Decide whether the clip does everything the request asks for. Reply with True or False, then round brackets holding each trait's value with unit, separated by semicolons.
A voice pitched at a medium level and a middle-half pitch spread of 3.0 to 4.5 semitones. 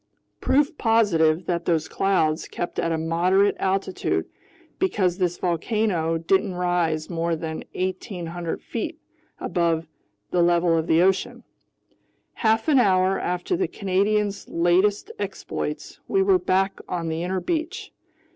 True (180 Hz; 3.3 semitones)